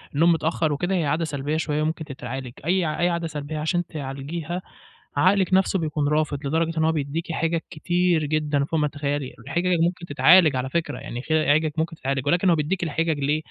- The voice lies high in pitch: No, medium, 155 Hz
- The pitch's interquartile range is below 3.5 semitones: Yes, average, 2.8 semitones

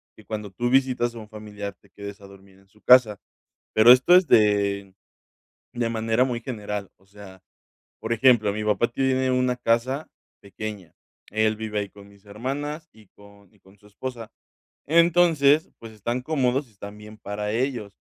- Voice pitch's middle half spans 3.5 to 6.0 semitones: Yes, average, 3.8 semitones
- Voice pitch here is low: Yes, low, 110 Hz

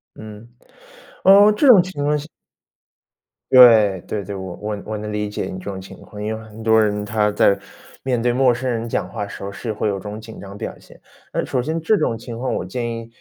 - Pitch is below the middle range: Yes, low, 110 Hz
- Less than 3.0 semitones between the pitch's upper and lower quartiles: No, average, 3.3 semitones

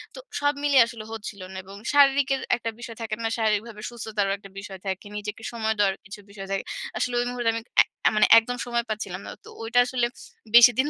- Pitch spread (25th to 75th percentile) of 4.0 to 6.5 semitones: No, average, 2.9 semitones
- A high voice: Yes, high, 225 Hz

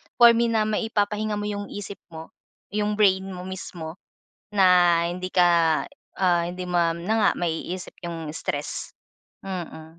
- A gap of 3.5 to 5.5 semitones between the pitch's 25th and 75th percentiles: No, average, 3.1 semitones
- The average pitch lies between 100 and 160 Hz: No, medium, 185 Hz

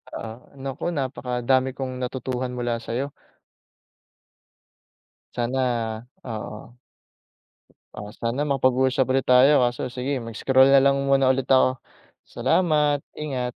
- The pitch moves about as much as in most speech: No, narrow, 1.7 semitones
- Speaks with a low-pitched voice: Yes, low, 130 Hz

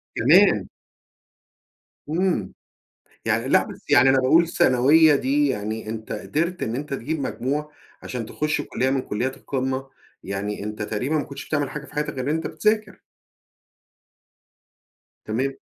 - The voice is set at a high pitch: No, low, 135 Hz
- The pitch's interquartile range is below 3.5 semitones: No, average, 3.8 semitones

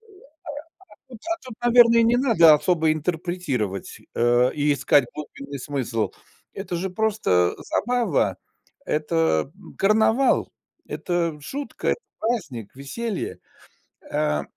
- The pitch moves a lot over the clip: Yes, wide, 8.3 semitones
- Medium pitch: Yes, medium, 170 Hz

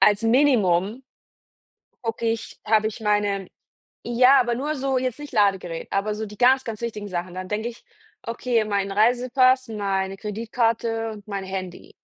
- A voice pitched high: Yes, high, 220 Hz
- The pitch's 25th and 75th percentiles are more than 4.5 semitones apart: No, average, 3.3 semitones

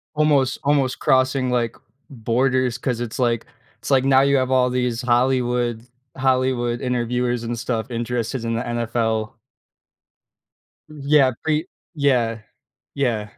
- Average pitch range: No, narrow, 2.0 semitones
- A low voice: Yes, low, 125 Hz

